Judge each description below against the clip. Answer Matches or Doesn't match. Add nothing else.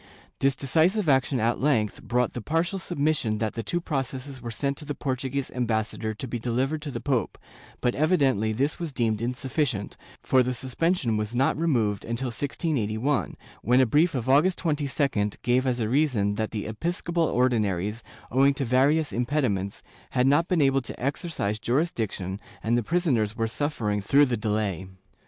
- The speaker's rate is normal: Matches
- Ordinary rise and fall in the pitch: Matches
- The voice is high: Doesn't match